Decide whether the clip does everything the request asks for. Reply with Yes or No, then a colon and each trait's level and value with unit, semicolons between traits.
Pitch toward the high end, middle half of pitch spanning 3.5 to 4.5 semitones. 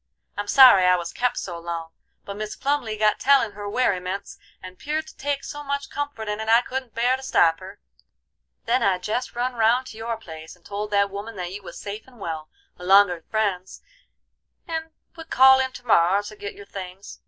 No: high, 210 Hz; average, 5.2 semitones